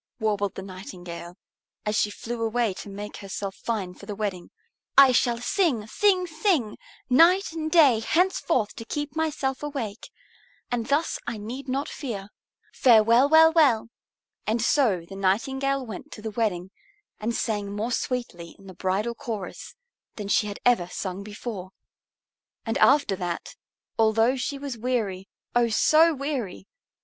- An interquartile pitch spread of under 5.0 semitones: No, wide, 5.4 semitones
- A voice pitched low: No, high, 230 Hz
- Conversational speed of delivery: Yes, average, 150 wpm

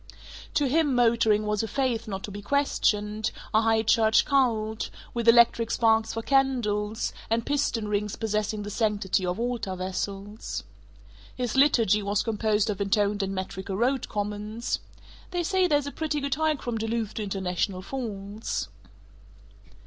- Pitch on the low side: No, high, 220 Hz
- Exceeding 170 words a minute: No, average, 150 wpm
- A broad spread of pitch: No, average, 2.9 semitones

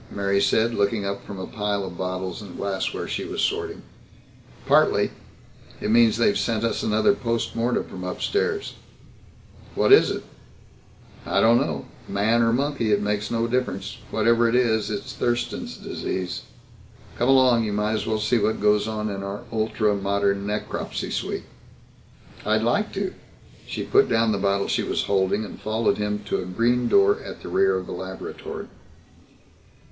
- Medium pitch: No, low, 110 Hz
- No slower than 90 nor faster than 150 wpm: No, average, 170 wpm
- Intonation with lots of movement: No, average, 2.8 semitones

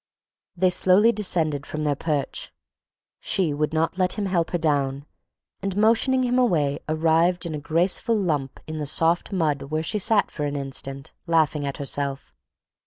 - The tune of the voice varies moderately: Yes, average, 4.3 semitones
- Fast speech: No, average, 170 wpm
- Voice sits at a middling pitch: Yes, medium, 160 Hz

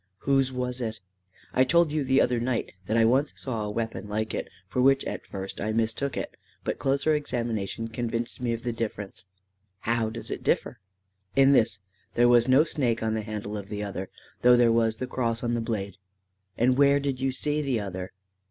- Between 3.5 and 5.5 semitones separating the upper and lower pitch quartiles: No, average, 3.0 semitones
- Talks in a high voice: No, low, 115 Hz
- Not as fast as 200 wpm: No, fast, 205 wpm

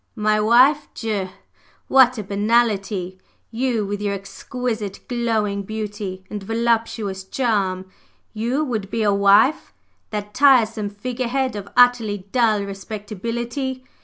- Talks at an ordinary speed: No, slow, 120 wpm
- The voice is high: Yes, high, 215 Hz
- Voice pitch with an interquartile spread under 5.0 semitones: Yes, average, 3.1 semitones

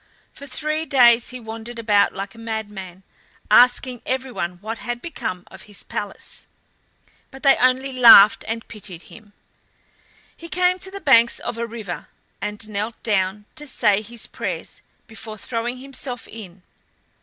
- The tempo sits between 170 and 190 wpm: No, average, 150 wpm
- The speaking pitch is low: No, high, 230 Hz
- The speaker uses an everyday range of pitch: Yes, average, 3.6 semitones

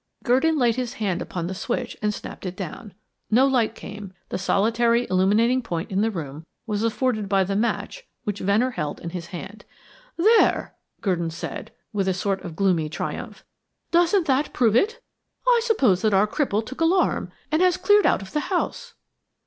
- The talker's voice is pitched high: Yes, high, 220 Hz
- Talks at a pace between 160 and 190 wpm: Yes, average, 180 wpm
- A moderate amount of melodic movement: No, wide, 5.7 semitones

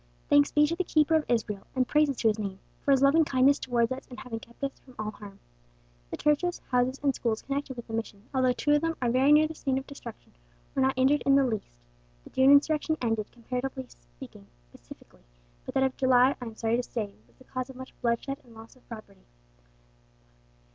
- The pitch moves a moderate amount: Yes, average, 3.6 semitones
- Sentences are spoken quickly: Yes, fast, 225 wpm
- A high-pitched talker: Yes, very high, 255 Hz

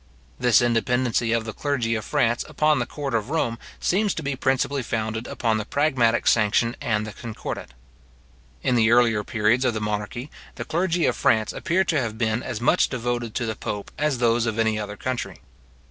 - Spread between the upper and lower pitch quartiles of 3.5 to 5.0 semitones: No, average, 3.0 semitones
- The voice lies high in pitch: No, low, 120 Hz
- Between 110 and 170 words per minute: No, average, 190 wpm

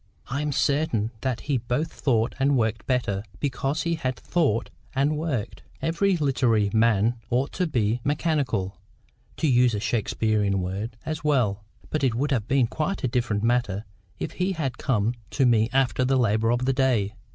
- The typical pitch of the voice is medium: No, low, 125 Hz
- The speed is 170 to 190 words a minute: Yes, average, 175 wpm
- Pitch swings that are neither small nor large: Yes, average, 4.4 semitones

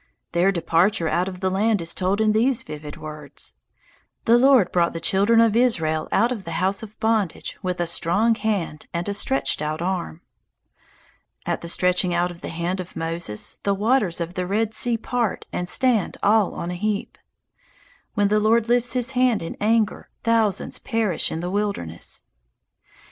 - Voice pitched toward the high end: Yes, high, 195 Hz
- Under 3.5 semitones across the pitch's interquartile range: No, average, 4.5 semitones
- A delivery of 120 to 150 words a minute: No, average, 180 wpm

